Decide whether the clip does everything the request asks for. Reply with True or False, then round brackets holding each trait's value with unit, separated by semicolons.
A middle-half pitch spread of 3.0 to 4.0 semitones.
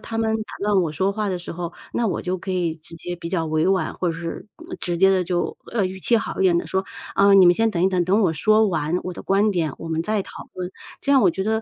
True (3.3 semitones)